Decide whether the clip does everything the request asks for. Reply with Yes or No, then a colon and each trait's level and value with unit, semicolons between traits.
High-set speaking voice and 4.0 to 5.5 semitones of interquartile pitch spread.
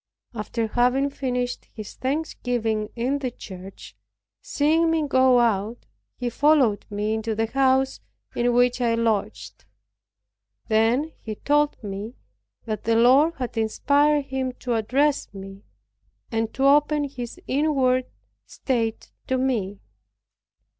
No: high, 245 Hz; average, 3.6 semitones